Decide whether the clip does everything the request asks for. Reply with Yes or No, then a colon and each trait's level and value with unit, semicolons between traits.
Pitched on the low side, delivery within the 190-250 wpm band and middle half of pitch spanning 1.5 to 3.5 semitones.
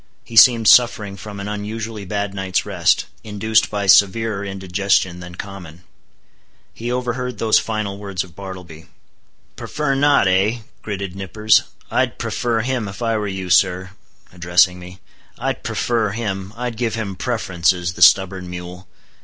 No: low, 100 Hz; average, 140 wpm; average, 3.2 semitones